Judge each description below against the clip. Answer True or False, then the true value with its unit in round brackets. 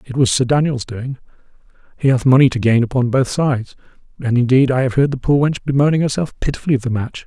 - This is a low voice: True (130 Hz)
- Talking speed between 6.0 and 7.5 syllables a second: True (6.5 syllables/s)